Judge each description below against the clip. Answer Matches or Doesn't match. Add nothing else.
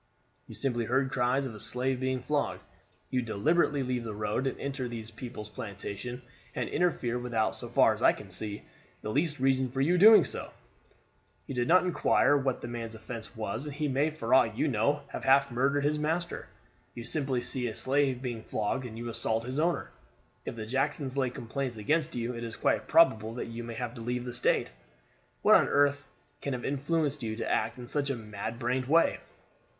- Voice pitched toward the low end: Matches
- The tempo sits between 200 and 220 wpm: Matches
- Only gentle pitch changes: Doesn't match